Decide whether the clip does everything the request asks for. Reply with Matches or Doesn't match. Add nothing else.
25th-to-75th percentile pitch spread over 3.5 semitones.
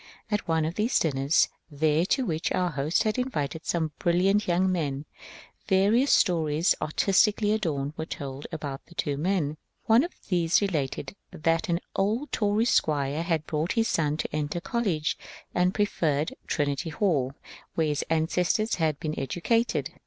Matches